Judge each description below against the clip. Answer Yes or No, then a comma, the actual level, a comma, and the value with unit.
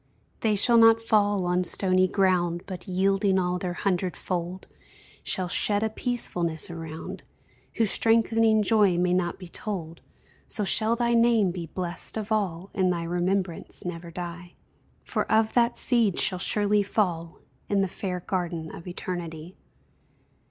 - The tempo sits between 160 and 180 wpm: No, average, 150 wpm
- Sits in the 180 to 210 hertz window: Yes, medium, 185 Hz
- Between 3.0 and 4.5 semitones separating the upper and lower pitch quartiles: Yes, average, 3.4 semitones